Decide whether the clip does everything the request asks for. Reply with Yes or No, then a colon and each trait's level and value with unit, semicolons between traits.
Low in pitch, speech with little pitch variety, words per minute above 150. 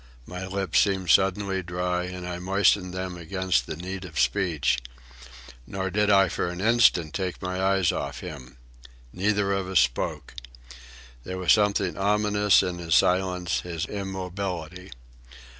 No: very low, 95 Hz; narrow, 1.7 semitones; average, 145 wpm